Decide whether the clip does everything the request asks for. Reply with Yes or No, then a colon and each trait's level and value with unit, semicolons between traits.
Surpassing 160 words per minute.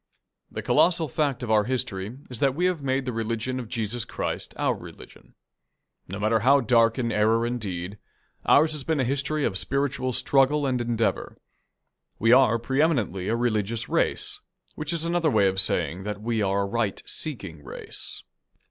Yes: average, 180 wpm